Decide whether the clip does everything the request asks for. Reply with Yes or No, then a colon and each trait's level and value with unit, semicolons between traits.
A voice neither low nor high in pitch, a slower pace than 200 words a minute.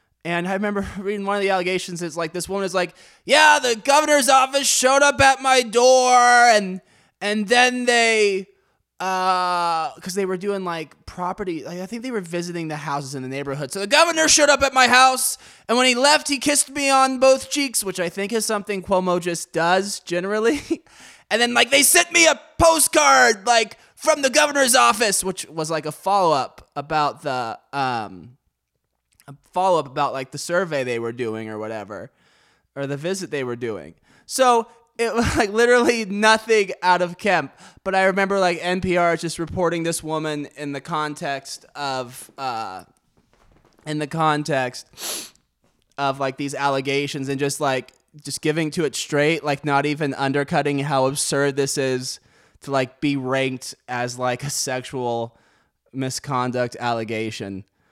Yes: medium, 180 Hz; average, 175 wpm